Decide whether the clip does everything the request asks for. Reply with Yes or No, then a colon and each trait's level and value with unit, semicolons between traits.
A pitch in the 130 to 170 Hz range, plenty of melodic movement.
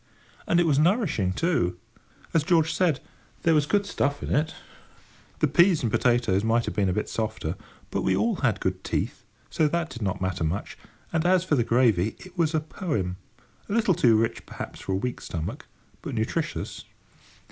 Yes: low, 135 Hz; wide, 8.6 semitones